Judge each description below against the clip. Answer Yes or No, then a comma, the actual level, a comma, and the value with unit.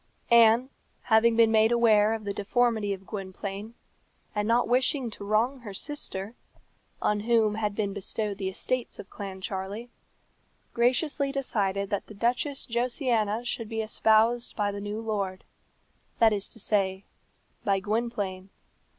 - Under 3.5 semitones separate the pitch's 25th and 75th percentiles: Yes, average, 2.7 semitones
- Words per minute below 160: Yes, average, 140 wpm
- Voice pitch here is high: Yes, high, 220 Hz